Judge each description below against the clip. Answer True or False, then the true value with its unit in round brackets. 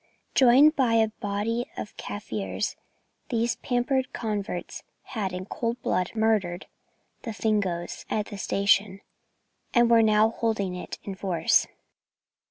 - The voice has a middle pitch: False (215 Hz)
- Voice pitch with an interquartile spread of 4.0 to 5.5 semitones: False (3.3 semitones)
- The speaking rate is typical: False (125 wpm)